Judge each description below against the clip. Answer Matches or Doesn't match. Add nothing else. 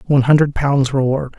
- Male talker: Matches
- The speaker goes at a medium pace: Matches